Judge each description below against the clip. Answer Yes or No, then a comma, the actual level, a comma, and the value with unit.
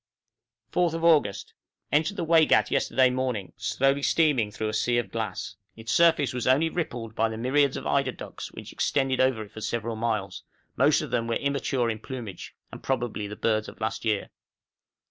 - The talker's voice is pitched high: No, low, 120 Hz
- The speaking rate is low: No, average, 185 wpm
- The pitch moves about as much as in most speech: Yes, average, 4.2 semitones